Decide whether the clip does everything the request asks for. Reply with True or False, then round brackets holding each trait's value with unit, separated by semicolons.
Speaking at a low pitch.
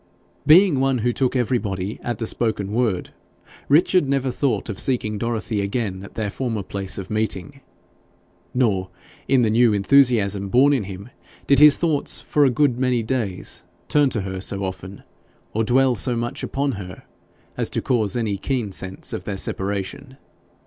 True (115 Hz)